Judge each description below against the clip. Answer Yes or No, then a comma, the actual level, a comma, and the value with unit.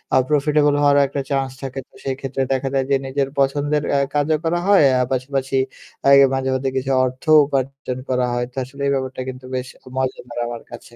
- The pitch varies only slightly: Yes, narrow, 1.5 semitones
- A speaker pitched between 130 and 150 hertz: Yes, low, 135 Hz